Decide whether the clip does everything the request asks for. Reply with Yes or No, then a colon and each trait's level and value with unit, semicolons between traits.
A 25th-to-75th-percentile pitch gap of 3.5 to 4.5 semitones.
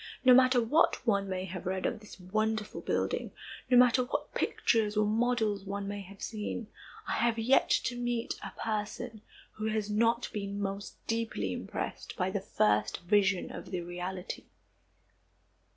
No: average, 2.9 semitones